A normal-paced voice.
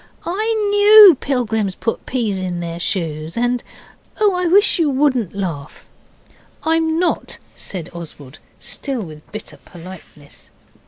No: slow, 125 wpm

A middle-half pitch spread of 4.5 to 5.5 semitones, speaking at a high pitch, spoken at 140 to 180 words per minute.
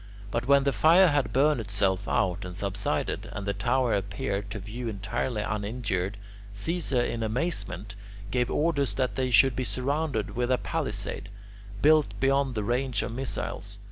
No: average, 4.9 semitones; low, 120 Hz; average, 160 wpm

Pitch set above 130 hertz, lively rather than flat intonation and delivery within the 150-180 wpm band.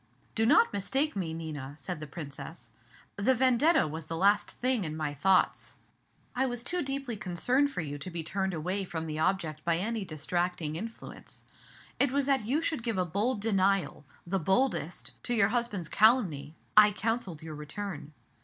Yes: high, 190 Hz; wide, 6.8 semitones; average, 175 wpm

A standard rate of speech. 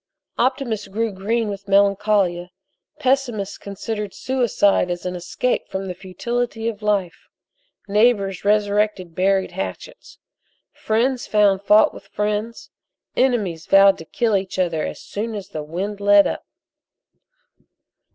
No: slow, 125 wpm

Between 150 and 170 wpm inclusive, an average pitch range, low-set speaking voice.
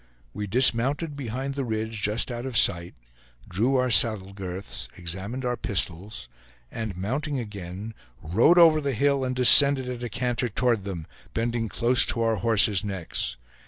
Yes: average, 160 wpm; average, 4.4 semitones; low, 115 Hz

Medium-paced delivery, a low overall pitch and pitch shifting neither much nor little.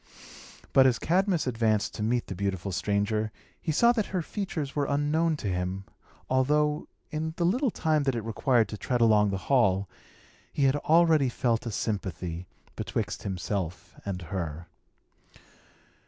No: average, 155 wpm; low, 120 Hz; wide, 7.4 semitones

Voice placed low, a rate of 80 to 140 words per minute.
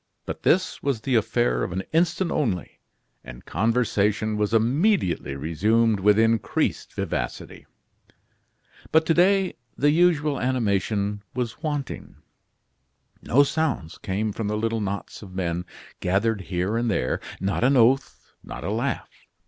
Yes: low, 110 Hz; slow, 135 wpm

